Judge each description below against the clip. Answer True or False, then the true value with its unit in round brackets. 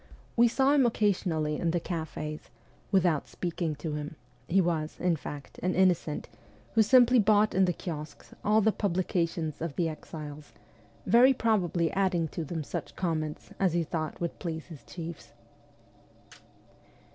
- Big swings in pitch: False (3.8 semitones)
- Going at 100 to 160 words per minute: True (155 wpm)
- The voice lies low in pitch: False (170 Hz)